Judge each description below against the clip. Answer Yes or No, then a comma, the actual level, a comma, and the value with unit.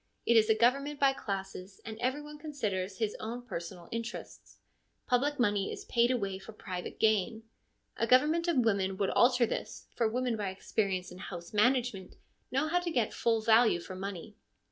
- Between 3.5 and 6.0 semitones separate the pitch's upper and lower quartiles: Yes, average, 4.5 semitones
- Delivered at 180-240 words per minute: Yes, average, 185 wpm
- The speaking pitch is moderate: No, high, 225 Hz